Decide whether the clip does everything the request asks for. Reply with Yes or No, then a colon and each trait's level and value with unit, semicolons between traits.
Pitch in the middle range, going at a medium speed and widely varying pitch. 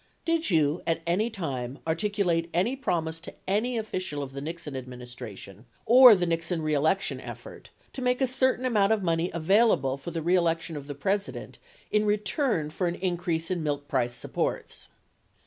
Yes: medium, 170 Hz; average, 170 wpm; wide, 5.7 semitones